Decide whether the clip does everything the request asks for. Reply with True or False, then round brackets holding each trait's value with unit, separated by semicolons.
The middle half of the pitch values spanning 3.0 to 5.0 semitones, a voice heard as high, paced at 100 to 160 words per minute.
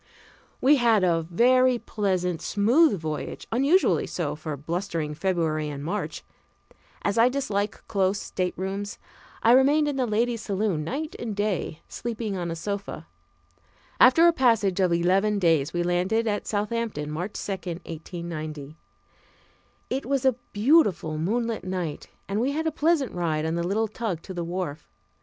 False (5.5 semitones; 200 Hz; 150 wpm)